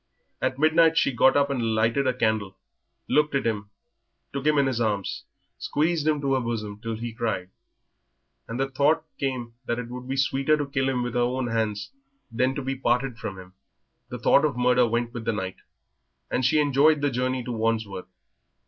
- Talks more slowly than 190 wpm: No, average, 200 wpm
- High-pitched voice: No, low, 125 Hz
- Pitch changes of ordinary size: Yes, average, 3.3 semitones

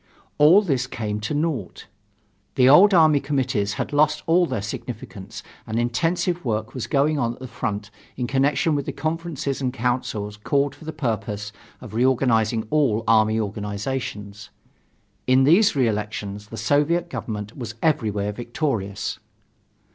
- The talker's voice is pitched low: Yes, low, 125 Hz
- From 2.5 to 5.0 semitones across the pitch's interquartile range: No, wide, 5.4 semitones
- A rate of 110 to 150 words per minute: Yes, average, 145 wpm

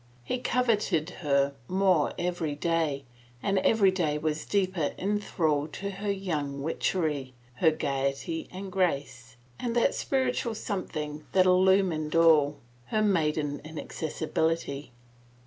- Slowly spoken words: Yes, slow, 125 wpm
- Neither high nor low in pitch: Yes, medium, 165 Hz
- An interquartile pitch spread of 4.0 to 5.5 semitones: Yes, average, 4.5 semitones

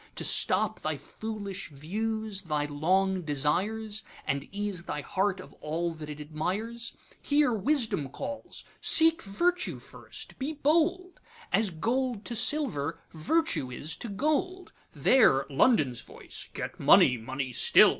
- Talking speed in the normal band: No, slow, 120 wpm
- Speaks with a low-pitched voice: No, high, 200 Hz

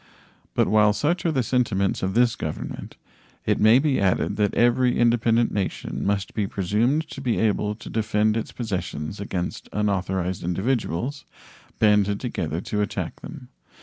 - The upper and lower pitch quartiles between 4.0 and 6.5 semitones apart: No, average, 3.4 semitones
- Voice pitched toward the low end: Yes, low, 105 Hz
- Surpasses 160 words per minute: No, average, 150 wpm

